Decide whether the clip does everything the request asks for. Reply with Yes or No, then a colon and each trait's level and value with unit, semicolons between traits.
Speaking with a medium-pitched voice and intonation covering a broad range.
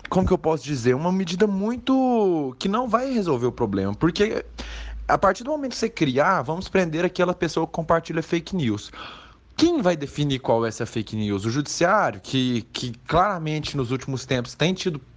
Yes: medium, 160 Hz; wide, 6.9 semitones